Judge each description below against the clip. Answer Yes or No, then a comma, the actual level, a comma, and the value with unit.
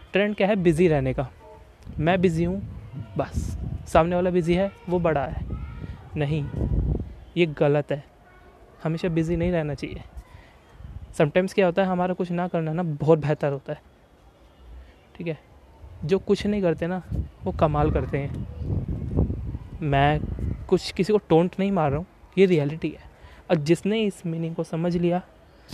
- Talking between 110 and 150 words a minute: No, average, 160 wpm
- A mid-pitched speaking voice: Yes, medium, 165 Hz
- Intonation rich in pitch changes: No, average, 4.1 semitones